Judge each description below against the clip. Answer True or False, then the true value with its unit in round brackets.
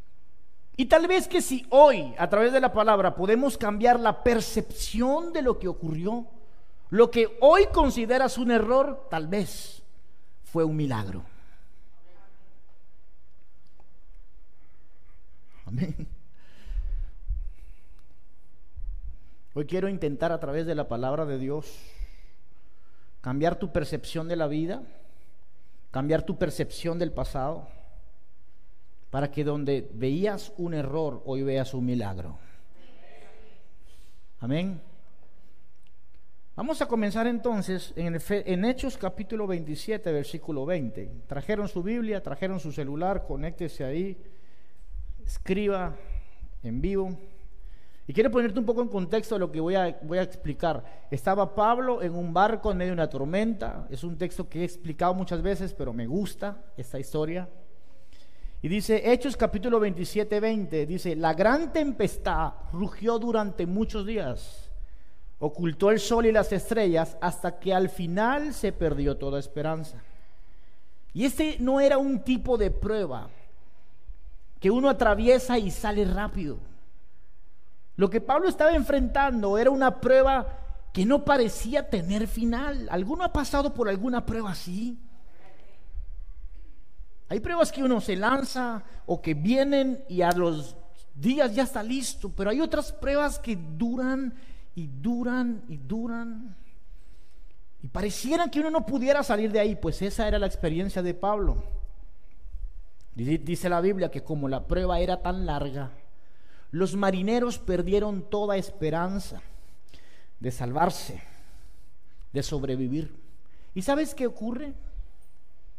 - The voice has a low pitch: False (180 Hz)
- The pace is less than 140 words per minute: True (130 wpm)